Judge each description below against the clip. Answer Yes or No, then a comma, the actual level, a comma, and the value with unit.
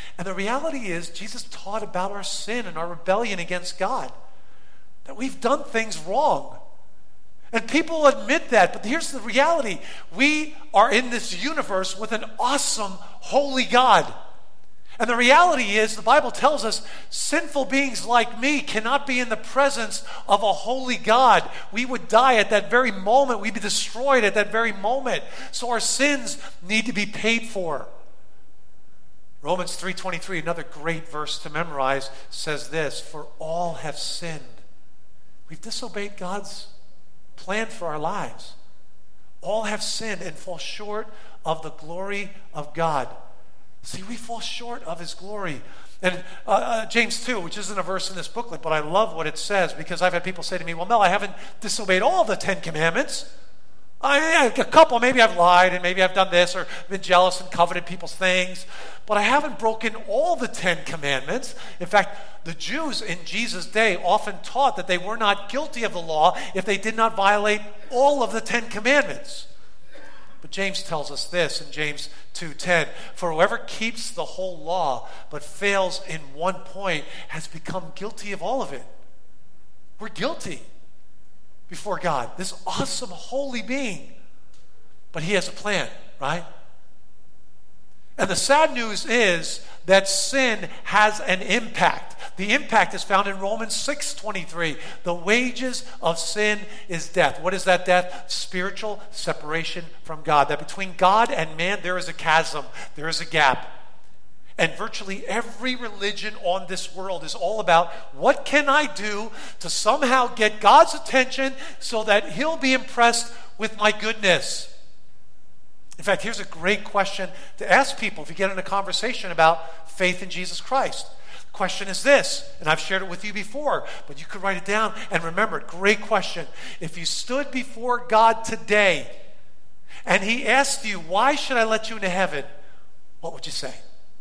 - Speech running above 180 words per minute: No, average, 170 wpm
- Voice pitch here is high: Yes, high, 200 Hz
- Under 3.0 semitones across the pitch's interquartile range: No, average, 5.2 semitones